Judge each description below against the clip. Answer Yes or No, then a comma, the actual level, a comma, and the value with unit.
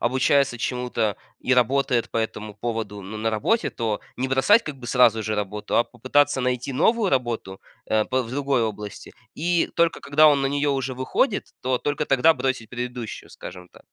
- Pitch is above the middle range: No, low, 125 Hz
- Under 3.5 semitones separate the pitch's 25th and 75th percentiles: No, average, 3.8 semitones